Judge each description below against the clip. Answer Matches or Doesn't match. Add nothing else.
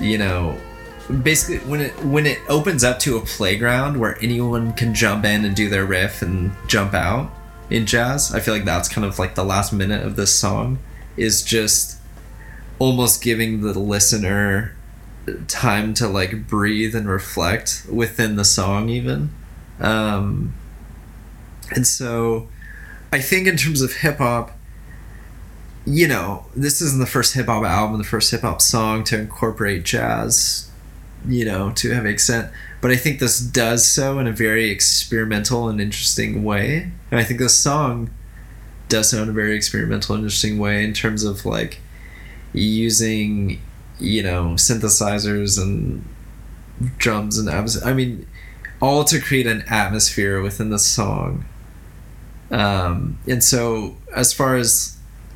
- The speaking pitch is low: Matches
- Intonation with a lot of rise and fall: Doesn't match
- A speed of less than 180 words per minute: Matches